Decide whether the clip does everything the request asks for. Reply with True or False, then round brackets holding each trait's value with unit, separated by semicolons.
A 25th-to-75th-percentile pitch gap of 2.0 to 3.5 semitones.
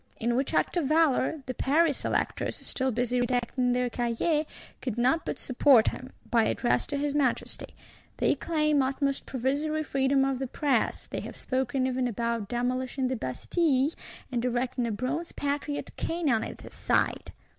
True (2.8 semitones)